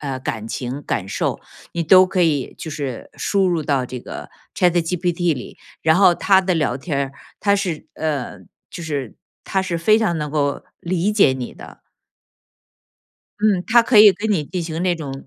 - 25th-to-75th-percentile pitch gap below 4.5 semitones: No, average, 4.8 semitones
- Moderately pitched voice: Yes, medium, 165 Hz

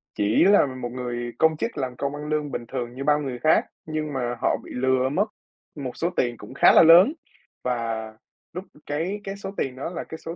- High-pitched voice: No, medium, 140 Hz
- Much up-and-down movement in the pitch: No, average, 4.4 semitones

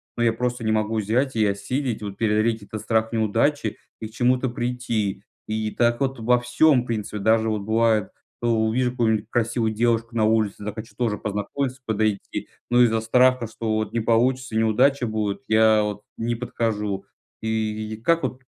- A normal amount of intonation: No, narrow, 2.1 semitones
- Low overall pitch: Yes, low, 110 Hz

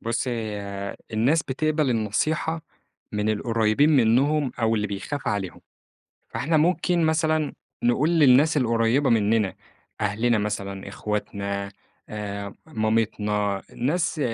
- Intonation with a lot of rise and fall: Yes, wide, 6.1 semitones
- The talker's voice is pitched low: Yes, low, 115 Hz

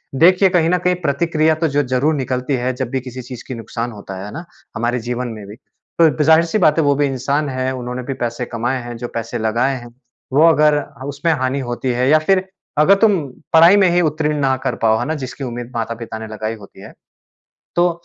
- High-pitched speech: No, low, 130 Hz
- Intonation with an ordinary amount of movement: Yes, average, 4.5 semitones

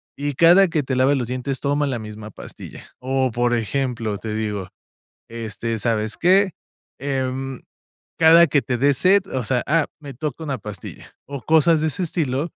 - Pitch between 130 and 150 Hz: Yes, low, 135 Hz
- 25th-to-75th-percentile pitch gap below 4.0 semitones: No, average, 4.5 semitones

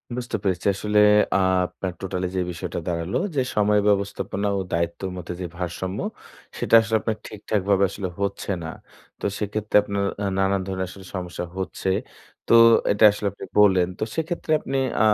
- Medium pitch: No, low, 100 Hz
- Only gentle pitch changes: Yes, narrow, 2.2 semitones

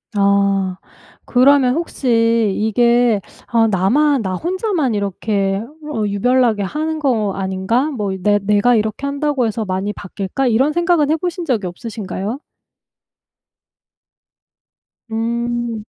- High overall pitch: Yes, high, 230 Hz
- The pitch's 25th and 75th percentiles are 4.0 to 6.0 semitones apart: Yes, average, 5.1 semitones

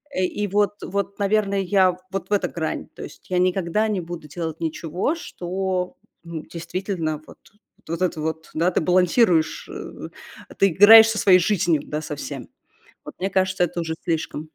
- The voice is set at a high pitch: No, medium, 180 Hz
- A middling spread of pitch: Yes, average, 3.2 semitones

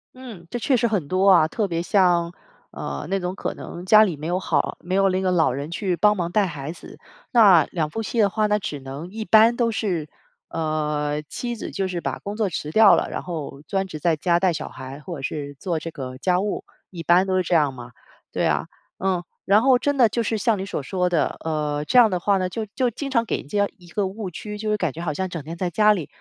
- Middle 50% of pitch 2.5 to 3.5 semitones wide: No, average, 4.7 semitones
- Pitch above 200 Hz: No, medium, 185 Hz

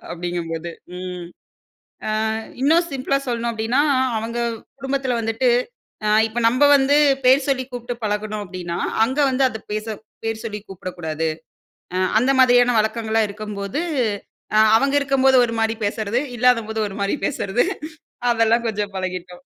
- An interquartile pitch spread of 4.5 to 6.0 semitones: No, average, 4.0 semitones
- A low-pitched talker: No, high, 225 Hz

